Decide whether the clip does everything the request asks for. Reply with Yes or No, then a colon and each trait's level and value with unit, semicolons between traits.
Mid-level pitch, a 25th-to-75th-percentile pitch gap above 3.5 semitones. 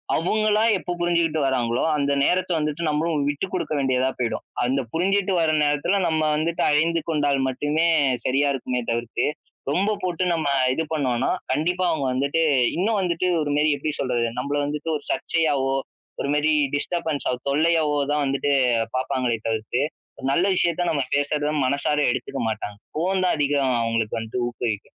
Yes: medium, 150 Hz; average, 4.0 semitones